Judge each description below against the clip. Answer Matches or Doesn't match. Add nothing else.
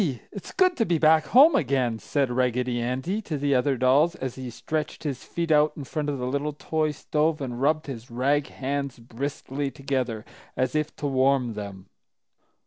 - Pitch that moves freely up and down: Doesn't match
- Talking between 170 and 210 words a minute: Matches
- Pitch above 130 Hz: Matches